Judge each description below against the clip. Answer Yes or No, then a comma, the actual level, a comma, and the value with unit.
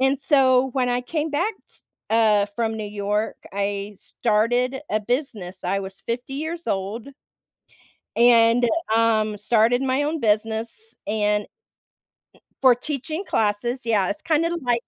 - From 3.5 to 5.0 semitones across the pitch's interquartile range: Yes, average, 4.1 semitones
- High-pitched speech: Yes, high, 235 Hz